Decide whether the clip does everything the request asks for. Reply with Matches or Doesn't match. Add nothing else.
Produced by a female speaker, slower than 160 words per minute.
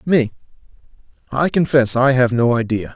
Doesn't match